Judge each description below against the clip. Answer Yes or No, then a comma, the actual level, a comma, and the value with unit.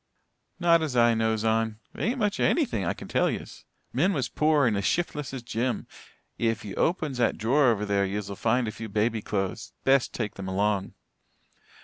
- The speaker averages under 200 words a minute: No, fast, 205 wpm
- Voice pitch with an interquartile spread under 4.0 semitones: No, average, 5.2 semitones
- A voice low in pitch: Yes, low, 115 Hz